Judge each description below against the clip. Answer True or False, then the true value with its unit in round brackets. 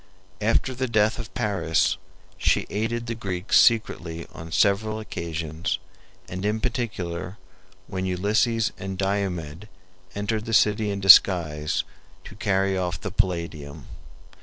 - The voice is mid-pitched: False (100 Hz)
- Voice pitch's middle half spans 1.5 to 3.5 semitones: False (3.9 semitones)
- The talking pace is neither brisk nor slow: False (125 wpm)